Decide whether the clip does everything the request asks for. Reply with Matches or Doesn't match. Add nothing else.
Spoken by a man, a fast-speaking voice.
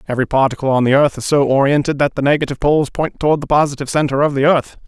Matches